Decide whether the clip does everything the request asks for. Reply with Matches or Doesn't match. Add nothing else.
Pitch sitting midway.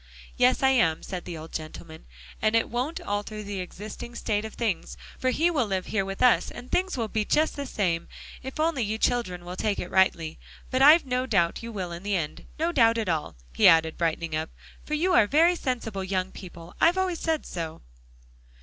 Doesn't match